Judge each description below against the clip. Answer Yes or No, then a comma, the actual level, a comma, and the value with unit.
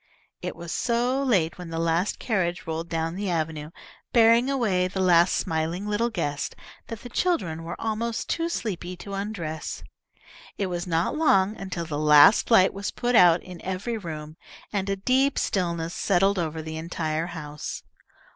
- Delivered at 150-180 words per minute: Yes, average, 165 wpm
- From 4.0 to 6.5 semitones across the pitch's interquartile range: Yes, average, 4.7 semitones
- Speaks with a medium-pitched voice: Yes, medium, 180 Hz